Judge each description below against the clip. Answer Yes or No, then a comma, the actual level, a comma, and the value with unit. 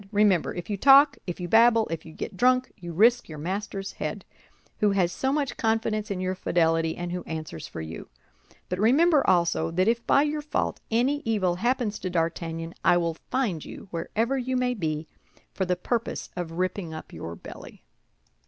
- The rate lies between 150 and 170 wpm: No, average, 190 wpm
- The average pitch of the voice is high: Yes, high, 195 Hz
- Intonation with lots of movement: Yes, wide, 6.0 semitones